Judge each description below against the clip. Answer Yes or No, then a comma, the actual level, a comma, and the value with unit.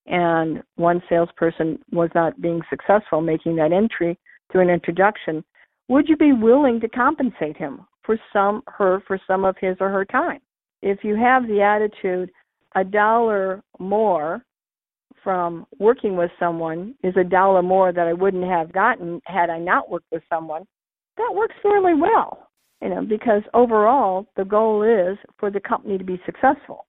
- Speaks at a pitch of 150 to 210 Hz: Yes, high, 190 Hz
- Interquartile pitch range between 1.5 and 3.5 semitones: No, average, 4.2 semitones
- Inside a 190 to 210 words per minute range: No, average, 165 wpm